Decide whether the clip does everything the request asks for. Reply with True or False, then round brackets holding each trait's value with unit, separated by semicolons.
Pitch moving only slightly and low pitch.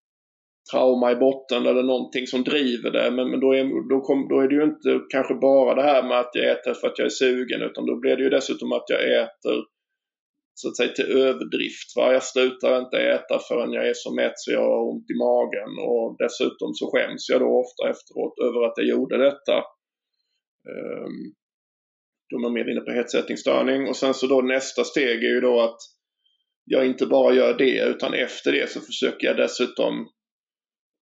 True (2.1 semitones; 130 Hz)